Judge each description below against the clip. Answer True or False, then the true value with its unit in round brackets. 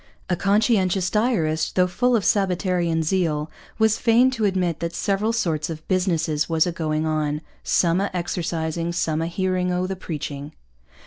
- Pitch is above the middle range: False (175 Hz)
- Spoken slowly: False (165 wpm)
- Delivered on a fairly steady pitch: False (3.3 semitones)